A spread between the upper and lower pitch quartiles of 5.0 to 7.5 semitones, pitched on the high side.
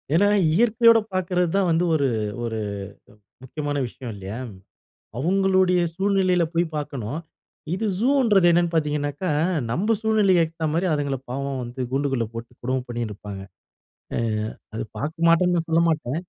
No: wide, 5.6 semitones; medium, 165 Hz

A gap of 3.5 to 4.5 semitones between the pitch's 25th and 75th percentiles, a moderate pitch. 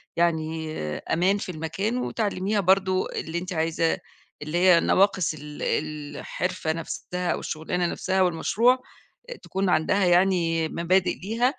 No: average, 2.9 semitones; medium, 180 Hz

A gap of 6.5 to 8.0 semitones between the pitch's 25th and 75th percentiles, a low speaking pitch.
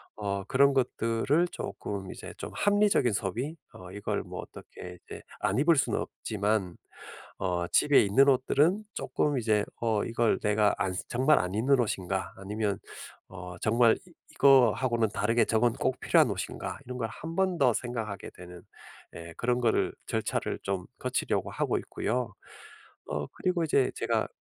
No: average, 5.1 semitones; low, 115 Hz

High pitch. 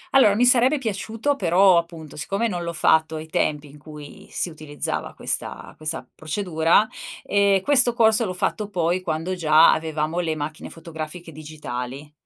No: medium, 165 Hz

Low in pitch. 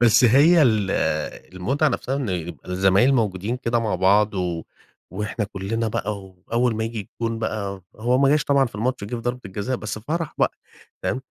Yes: low, 110 Hz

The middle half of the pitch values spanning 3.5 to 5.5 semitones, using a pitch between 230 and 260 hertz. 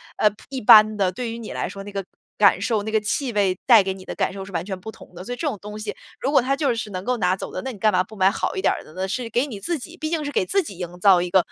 No: average, 4.6 semitones; high, 210 Hz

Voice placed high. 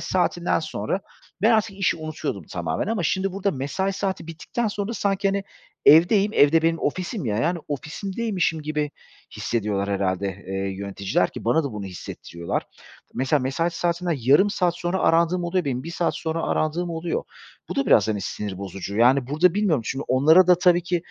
No: medium, 165 Hz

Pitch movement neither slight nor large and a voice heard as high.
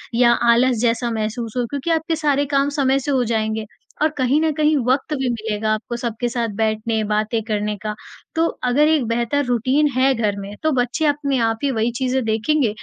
Yes: average, 4.1 semitones; high, 245 Hz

